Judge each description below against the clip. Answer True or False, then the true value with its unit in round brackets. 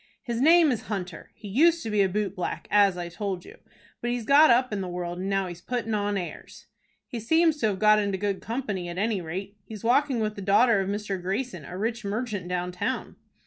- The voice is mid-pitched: False (205 Hz)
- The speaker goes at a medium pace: False (235 wpm)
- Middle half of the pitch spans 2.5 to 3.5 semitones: False (3.9 semitones)